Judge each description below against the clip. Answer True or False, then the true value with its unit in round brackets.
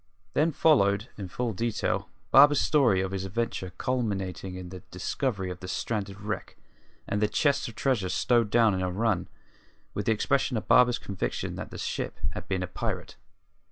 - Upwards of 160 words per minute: True (180 wpm)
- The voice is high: False (105 Hz)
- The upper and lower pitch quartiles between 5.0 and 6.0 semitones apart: False (4.5 semitones)